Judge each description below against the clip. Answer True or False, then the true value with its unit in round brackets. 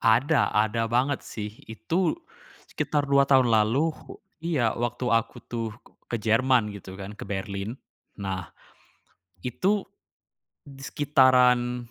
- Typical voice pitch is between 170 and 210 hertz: False (120 Hz)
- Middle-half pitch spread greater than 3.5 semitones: True (4.0 semitones)